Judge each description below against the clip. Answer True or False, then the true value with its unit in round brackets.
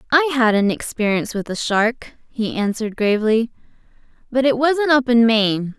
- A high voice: True (235 Hz)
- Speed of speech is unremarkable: True (165 wpm)